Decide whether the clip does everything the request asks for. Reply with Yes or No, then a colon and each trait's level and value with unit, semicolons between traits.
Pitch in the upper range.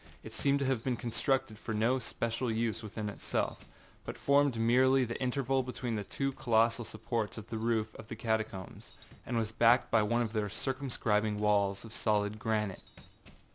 No: low, 115 Hz